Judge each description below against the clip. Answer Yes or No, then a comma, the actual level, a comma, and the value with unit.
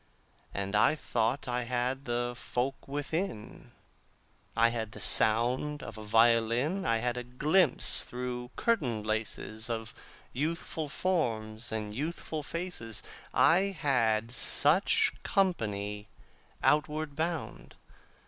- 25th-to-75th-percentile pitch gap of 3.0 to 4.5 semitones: No, average, 5.3 semitones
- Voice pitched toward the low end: Yes, low, 125 Hz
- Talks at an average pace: No, slow, 110 wpm